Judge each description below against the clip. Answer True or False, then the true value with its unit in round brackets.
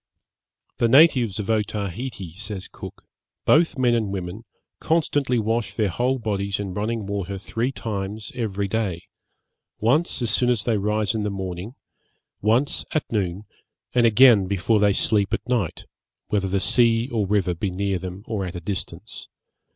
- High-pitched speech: False (105 Hz)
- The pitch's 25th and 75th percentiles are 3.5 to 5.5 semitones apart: False (3.1 semitones)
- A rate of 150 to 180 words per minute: True (160 wpm)